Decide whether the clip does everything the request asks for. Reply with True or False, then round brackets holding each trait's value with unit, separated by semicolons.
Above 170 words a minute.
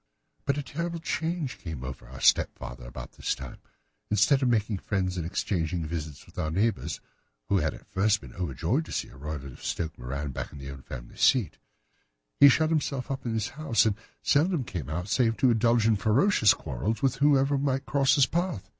True (200 wpm)